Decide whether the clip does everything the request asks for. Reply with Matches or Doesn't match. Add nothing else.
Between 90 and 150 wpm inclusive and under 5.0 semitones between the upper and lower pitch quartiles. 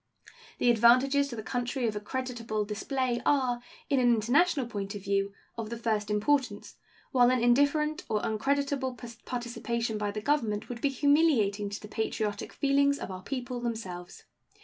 Doesn't match